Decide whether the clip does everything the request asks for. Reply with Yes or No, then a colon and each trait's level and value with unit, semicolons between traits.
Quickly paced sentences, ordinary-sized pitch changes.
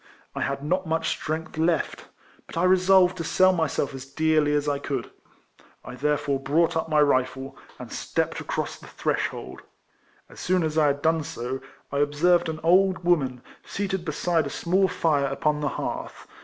No: average, 175 wpm; average, 3.5 semitones